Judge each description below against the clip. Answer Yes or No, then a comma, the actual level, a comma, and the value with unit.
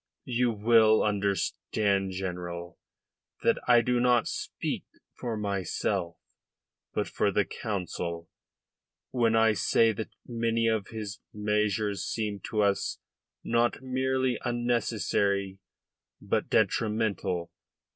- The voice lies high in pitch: No, low, 105 Hz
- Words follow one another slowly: Yes, slow, 105 wpm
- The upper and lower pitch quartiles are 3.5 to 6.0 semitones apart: No, average, 2.9 semitones